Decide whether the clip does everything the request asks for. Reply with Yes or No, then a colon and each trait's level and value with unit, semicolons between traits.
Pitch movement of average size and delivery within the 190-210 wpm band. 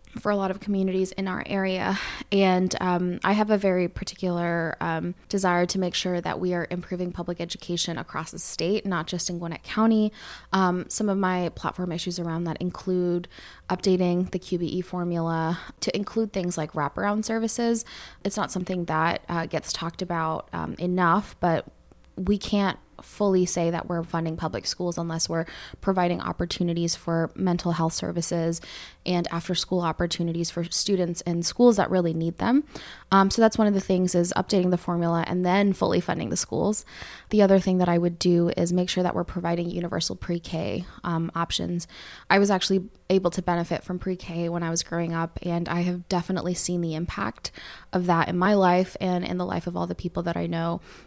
No: narrow, 1.8 semitones; average, 195 wpm